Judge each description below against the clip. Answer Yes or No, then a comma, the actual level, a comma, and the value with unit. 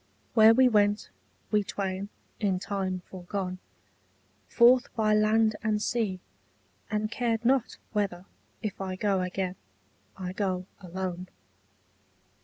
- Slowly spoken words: Yes, slow, 115 wpm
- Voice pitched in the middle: No, high, 205 Hz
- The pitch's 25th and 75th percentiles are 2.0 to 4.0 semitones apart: Yes, average, 2.7 semitones